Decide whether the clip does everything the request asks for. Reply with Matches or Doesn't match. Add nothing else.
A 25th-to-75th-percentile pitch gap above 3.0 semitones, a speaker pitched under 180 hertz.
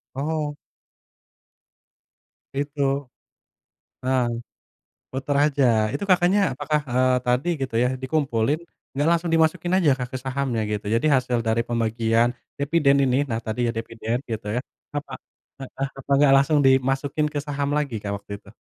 Matches